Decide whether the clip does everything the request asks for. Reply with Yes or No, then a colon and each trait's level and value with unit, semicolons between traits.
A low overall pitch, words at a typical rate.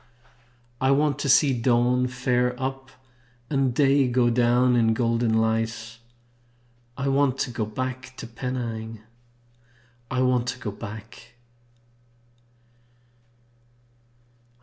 No: low, 125 Hz; slow, 105 wpm